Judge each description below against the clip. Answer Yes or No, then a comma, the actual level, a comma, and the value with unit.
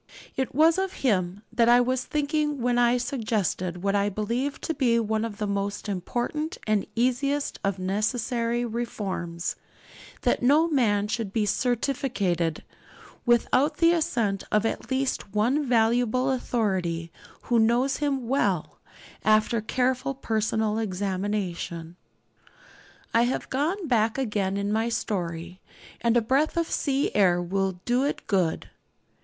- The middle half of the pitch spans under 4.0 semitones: No, average, 4.4 semitones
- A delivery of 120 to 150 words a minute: Yes, average, 140 wpm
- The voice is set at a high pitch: Yes, high, 230 Hz